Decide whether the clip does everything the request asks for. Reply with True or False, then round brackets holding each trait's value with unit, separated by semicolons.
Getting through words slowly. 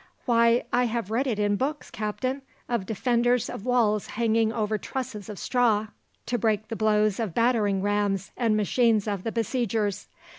False (160 wpm)